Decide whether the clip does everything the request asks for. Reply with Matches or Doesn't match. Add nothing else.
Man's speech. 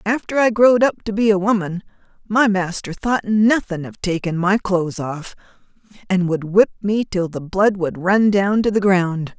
Doesn't match